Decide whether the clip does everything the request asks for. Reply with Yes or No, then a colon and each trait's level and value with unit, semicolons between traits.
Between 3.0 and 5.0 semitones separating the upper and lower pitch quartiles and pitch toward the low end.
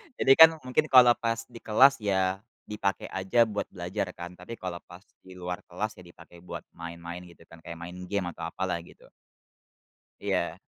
Yes: average, 4.0 semitones; very low, 95 Hz